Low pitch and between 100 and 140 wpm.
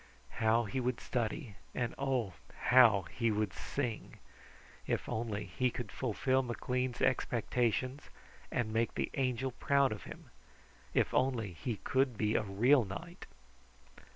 Yes: low, 120 Hz; slow, 135 wpm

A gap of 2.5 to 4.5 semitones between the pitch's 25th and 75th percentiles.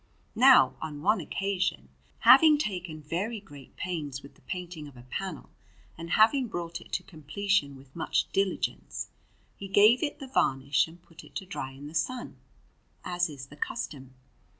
No: wide, 5.5 semitones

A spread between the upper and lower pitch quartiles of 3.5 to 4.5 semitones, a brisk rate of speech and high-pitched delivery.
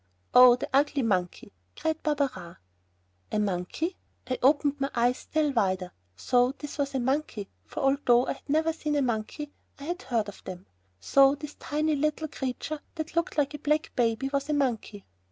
No: average, 3.9 semitones; average, 180 wpm; very high, 275 Hz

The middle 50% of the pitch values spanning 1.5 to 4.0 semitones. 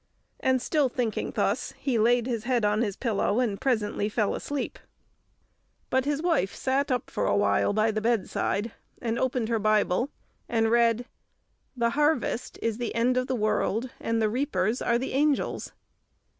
Yes: average, 3.1 semitones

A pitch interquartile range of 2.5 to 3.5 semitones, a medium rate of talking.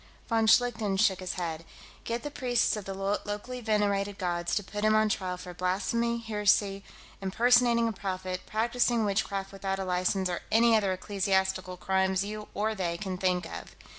Yes: average, 2.8 semitones; average, 170 wpm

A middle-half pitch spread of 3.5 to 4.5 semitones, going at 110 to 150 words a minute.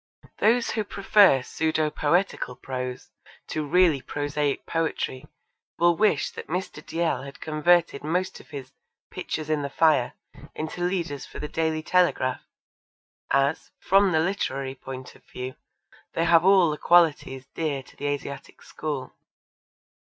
Yes: average, 3.9 semitones; average, 140 wpm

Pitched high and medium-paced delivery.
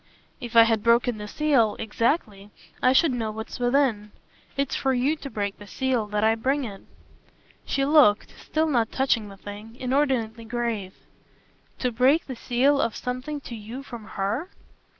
Yes: high, 240 Hz; average, 170 wpm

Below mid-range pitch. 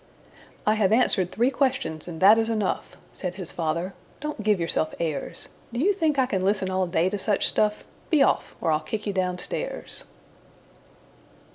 No: high, 200 Hz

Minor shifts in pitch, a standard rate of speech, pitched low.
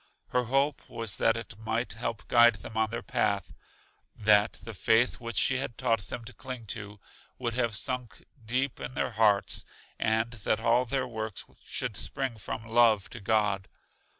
Yes: narrow, 2.0 semitones; average, 175 wpm; low, 115 Hz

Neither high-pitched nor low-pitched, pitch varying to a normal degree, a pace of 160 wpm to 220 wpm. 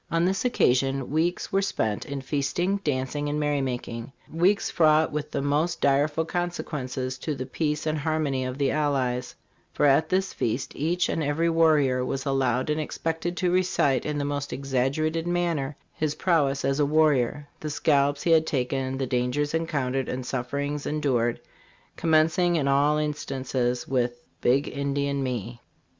Yes: medium, 145 Hz; average, 3.1 semitones; average, 165 wpm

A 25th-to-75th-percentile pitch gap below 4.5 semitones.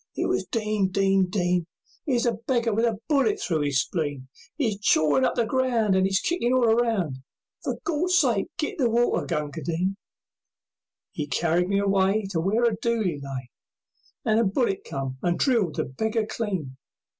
No: wide, 5.6 semitones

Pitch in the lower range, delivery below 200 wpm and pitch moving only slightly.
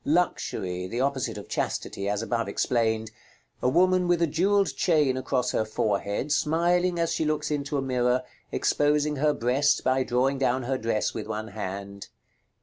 No: low, 130 Hz; average, 170 wpm; average, 5.0 semitones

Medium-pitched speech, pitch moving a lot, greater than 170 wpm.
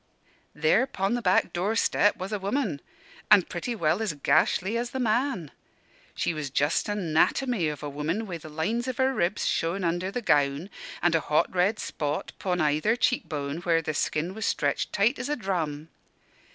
Yes: medium, 180 Hz; wide, 6.1 semitones; average, 190 wpm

